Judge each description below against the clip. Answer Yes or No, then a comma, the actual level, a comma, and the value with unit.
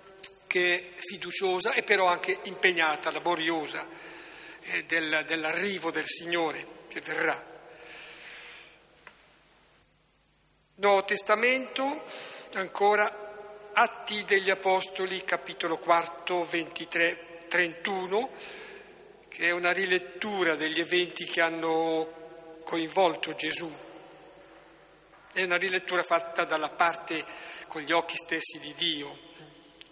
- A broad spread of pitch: No, average, 2.7 semitones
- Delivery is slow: Yes, slow, 90 wpm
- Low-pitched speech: No, medium, 175 Hz